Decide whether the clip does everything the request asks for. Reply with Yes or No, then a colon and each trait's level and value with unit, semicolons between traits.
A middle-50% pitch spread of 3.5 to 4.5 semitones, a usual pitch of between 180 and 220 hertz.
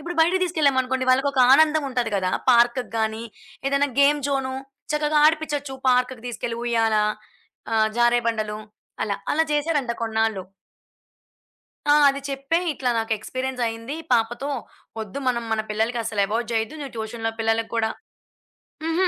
No: average, 4.0 semitones; high, 245 Hz